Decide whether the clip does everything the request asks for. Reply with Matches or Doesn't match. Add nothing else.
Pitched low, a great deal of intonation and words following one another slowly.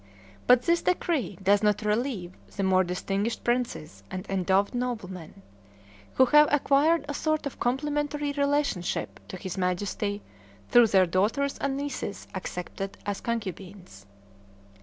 Doesn't match